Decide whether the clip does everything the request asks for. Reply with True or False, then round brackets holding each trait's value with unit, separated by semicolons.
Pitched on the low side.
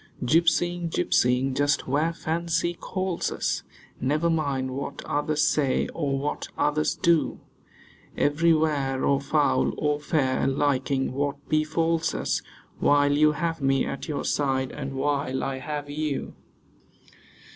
False (145 Hz)